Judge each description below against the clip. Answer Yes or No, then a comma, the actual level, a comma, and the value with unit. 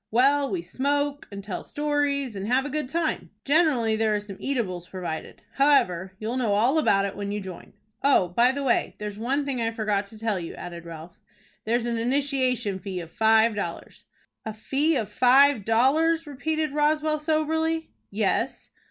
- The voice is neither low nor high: No, high, 245 Hz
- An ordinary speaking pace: Yes, average, 180 wpm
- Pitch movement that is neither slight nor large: No, wide, 5.8 semitones